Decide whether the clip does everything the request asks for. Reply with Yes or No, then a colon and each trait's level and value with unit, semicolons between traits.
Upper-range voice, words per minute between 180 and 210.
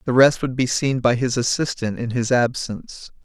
No: low, 125 Hz; fast, 205 wpm